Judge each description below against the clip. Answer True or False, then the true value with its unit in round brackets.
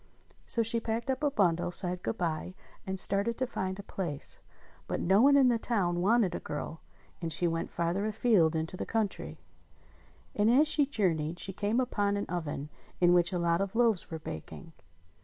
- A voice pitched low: False (190 Hz)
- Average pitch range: True (4.8 semitones)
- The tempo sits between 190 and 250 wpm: True (195 wpm)